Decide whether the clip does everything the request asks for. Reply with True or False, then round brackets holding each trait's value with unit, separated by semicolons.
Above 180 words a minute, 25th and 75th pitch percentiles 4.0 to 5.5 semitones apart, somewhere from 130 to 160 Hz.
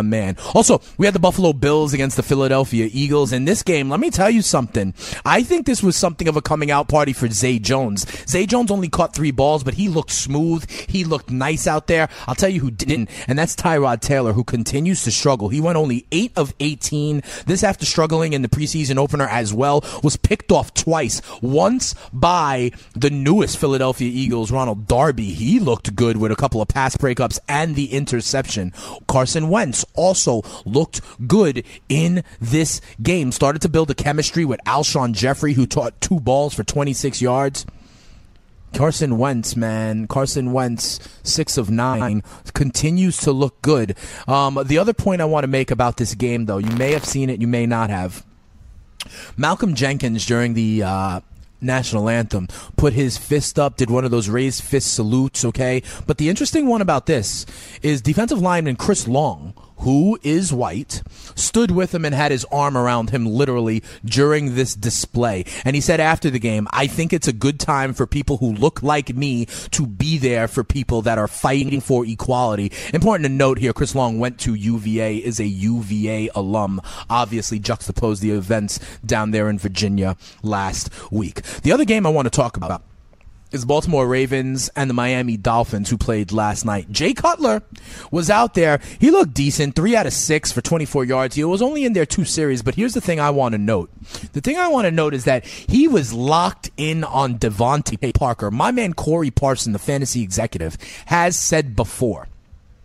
True (190 wpm; 5.0 semitones; 135 Hz)